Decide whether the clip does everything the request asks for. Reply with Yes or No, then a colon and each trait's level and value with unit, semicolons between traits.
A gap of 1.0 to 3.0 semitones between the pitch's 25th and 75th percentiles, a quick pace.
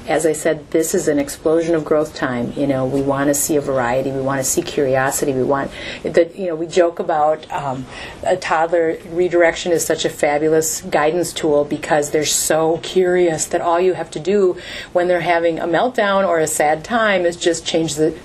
Yes: average, 2.7 semitones; fast, 210 wpm